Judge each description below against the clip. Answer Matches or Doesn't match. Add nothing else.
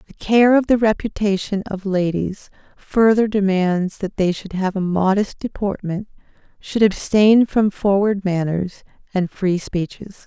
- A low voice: Doesn't match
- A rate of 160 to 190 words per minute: Doesn't match